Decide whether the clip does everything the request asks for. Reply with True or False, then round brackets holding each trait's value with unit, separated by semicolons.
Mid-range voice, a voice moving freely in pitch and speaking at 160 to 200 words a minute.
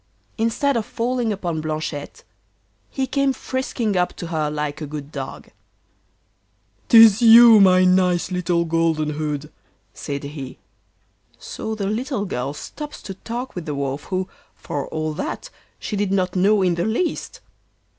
False (180 Hz; 6.4 semitones; 150 wpm)